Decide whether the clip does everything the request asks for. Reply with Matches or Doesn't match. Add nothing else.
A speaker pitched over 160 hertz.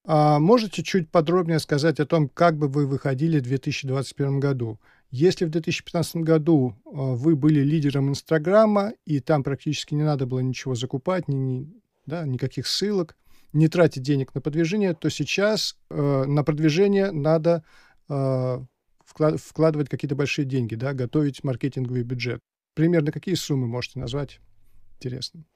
Doesn't match